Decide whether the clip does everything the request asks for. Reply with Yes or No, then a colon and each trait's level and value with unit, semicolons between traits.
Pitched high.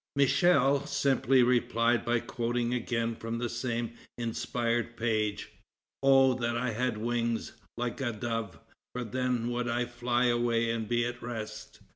No: low, 120 Hz